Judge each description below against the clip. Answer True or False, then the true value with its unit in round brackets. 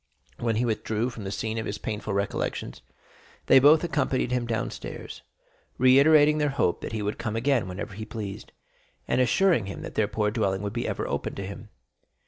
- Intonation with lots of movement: False (3.9 semitones)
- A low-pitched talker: True (110 Hz)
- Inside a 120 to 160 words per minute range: False (195 wpm)